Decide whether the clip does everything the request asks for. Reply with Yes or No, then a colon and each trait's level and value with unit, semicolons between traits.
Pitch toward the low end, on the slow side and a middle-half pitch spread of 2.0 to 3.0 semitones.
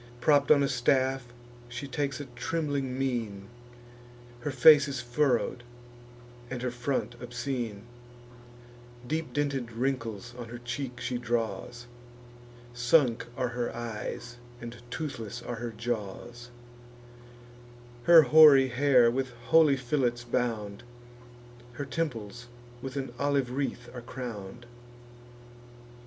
Yes: low, 125 Hz; slow, 115 wpm; narrow, 2.4 semitones